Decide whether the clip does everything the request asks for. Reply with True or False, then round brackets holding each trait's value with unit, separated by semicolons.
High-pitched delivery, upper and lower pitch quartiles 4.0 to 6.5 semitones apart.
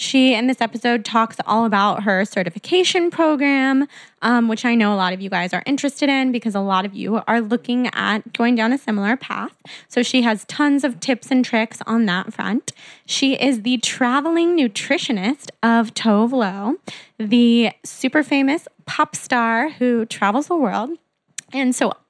False (240 Hz; 3.6 semitones)